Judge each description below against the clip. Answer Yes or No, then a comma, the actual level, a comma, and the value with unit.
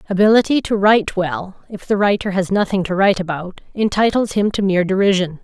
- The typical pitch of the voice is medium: No, high, 195 Hz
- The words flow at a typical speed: Yes, average, 190 wpm